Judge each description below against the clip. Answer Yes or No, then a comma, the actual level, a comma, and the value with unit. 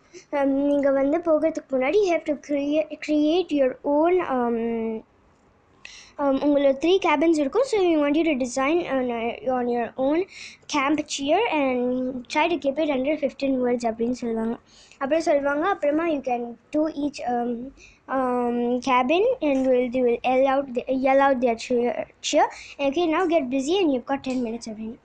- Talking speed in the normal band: No, fast, 140 wpm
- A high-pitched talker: Yes, very high, 275 Hz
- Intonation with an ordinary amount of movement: Yes, average, 3.7 semitones